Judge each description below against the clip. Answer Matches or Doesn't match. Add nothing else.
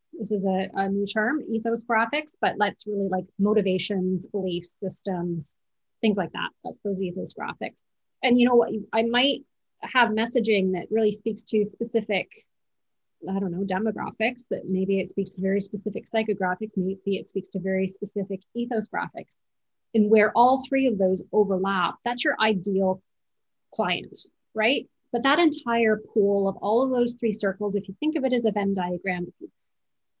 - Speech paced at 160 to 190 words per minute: Matches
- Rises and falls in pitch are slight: Doesn't match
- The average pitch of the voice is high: Matches